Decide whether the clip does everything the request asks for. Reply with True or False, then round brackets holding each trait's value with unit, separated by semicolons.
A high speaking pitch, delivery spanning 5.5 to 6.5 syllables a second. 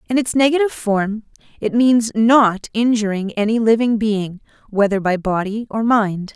False (220 Hz; 4.6 syllables/s)